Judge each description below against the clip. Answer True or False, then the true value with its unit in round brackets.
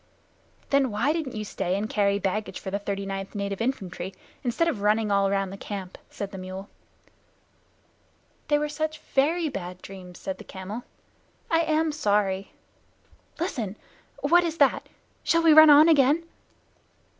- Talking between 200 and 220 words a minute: False (155 wpm)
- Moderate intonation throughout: False (7.3 semitones)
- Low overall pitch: False (210 Hz)